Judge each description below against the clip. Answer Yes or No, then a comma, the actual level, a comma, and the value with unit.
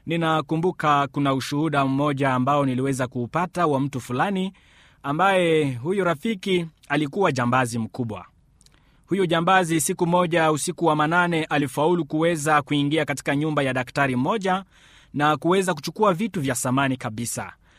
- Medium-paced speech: Yes, average, 130 wpm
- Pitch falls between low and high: Yes, medium, 150 Hz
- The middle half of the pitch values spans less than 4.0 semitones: No, average, 4.3 semitones